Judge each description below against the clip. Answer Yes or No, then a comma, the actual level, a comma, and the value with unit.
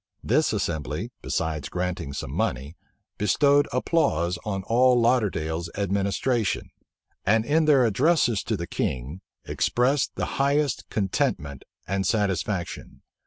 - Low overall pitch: Yes, low, 100 Hz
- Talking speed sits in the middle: No, slow, 115 wpm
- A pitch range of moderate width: No, wide, 6.7 semitones